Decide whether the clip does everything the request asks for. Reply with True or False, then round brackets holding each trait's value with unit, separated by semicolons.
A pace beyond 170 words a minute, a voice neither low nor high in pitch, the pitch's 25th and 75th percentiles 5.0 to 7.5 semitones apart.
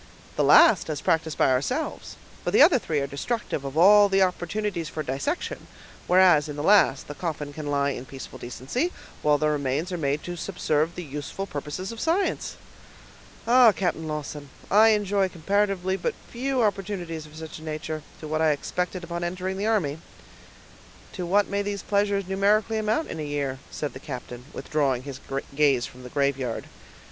True (180 wpm; 165 Hz; 5.5 semitones)